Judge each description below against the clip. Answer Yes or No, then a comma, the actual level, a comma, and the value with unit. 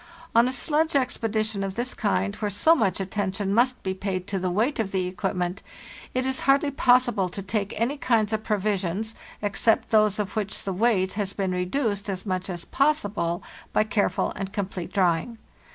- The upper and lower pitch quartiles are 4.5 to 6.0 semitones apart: No, average, 3.6 semitones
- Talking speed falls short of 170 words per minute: No, average, 185 wpm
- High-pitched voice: Yes, high, 205 Hz